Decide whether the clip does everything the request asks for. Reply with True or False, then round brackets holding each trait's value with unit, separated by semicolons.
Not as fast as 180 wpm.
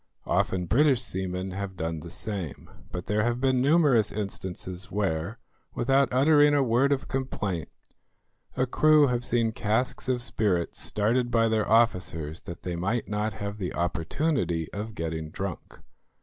True (150 wpm)